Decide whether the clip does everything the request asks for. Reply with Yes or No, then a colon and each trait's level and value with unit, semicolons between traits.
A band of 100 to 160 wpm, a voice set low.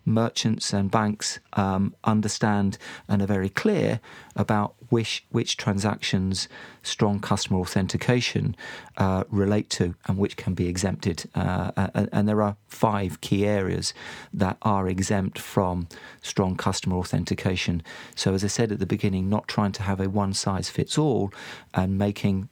Yes: average, 150 wpm; low, 100 Hz